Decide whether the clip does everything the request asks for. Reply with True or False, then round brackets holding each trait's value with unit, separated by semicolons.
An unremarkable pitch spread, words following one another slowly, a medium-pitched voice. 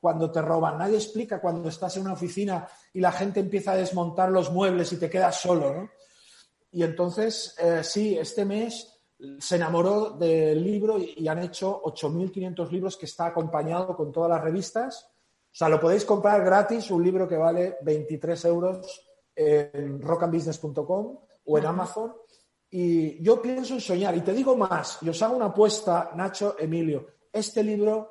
False (3.8 semitones; 175 wpm; 180 Hz)